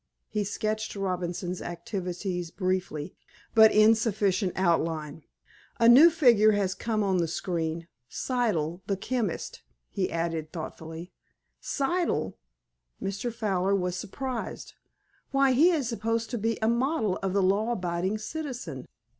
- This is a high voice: Yes, high, 195 Hz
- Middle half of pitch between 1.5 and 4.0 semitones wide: No, average, 4.6 semitones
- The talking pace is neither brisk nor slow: No, slow, 125 wpm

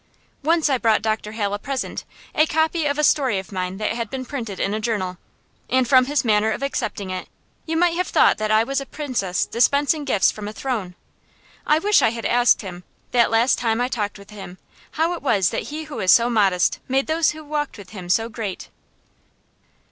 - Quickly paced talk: Yes, fast, 215 wpm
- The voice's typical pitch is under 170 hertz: No, high, 235 Hz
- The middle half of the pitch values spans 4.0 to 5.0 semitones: No, wide, 5.6 semitones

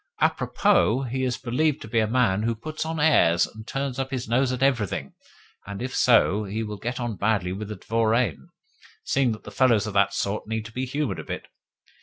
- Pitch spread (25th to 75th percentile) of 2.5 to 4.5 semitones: Yes, average, 3.6 semitones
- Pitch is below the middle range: Yes, low, 115 Hz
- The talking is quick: Yes, fast, 215 wpm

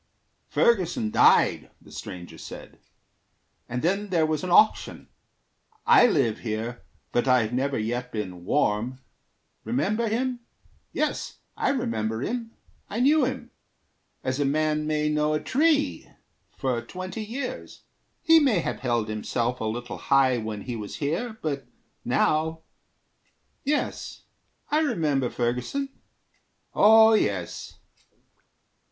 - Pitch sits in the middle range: Yes, medium, 150 Hz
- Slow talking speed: Yes, slow, 120 wpm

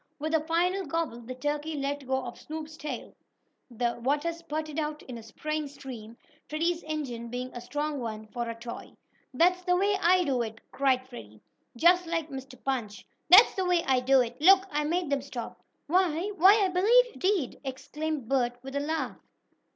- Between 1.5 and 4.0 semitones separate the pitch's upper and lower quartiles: No, average, 4.9 semitones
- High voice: Yes, very high, 295 Hz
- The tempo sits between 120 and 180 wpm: No, average, 190 wpm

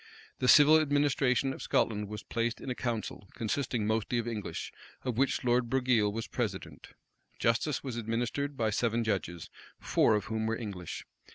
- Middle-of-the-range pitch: No, low, 115 Hz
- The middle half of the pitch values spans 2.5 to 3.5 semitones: Yes, average, 3.0 semitones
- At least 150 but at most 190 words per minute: Yes, average, 165 wpm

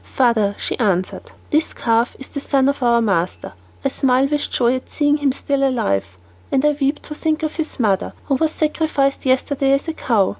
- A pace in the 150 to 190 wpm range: No, average, 200 wpm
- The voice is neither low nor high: No, very high, 270 Hz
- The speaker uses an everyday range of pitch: Yes, average, 3.9 semitones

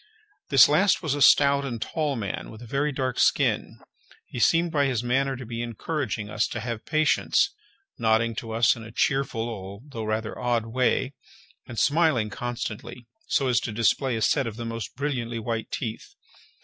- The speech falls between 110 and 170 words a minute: No, average, 180 wpm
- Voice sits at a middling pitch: No, low, 120 Hz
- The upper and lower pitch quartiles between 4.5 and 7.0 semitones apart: No, average, 3.5 semitones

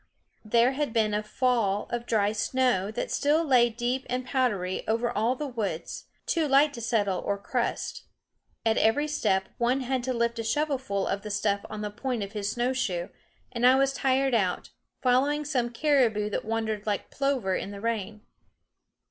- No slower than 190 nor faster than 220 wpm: No, average, 180 wpm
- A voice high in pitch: Yes, high, 235 Hz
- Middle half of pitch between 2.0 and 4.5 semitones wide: Yes, average, 3.8 semitones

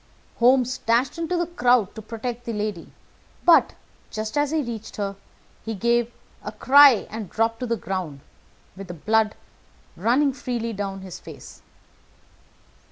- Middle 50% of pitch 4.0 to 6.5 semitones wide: No, average, 3.2 semitones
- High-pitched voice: Yes, high, 230 Hz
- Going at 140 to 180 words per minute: Yes, average, 150 wpm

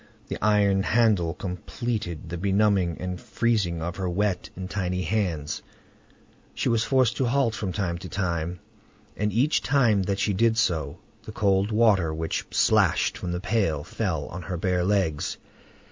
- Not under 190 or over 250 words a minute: No, average, 160 wpm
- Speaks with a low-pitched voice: Yes, very low, 95 Hz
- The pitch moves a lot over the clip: No, average, 3.6 semitones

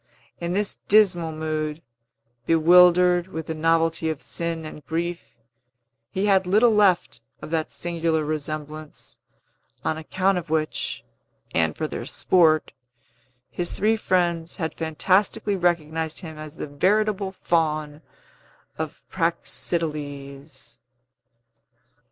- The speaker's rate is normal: No, slow, 110 wpm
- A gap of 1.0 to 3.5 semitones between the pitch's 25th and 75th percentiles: Yes, average, 2.7 semitones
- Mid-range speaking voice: Yes, medium, 165 Hz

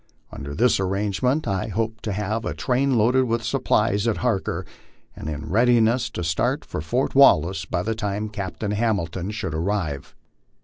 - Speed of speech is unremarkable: Yes, average, 170 wpm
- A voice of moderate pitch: No, low, 105 Hz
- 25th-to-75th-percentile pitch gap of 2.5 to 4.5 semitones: Yes, average, 3.9 semitones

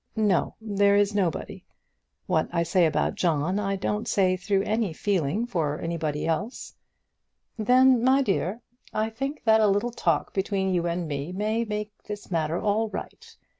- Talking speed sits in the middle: Yes, average, 165 wpm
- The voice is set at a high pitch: Yes, high, 200 Hz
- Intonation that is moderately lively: Yes, average, 4.1 semitones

